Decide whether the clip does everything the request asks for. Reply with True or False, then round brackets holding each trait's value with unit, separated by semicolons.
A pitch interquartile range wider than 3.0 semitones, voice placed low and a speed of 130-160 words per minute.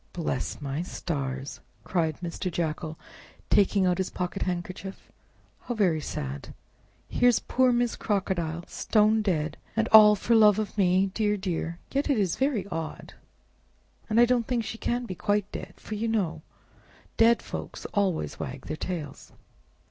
False (4.7 semitones; 190 Hz; 150 wpm)